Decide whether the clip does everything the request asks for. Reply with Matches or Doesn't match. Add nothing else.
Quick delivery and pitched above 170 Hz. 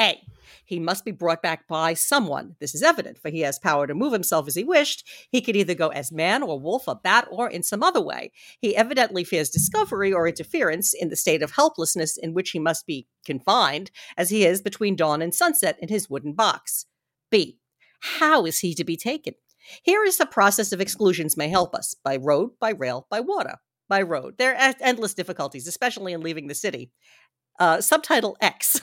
Matches